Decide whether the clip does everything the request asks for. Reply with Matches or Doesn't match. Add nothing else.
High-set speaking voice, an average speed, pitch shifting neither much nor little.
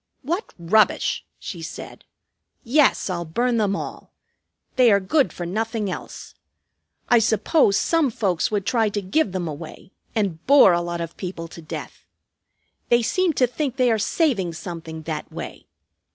Doesn't match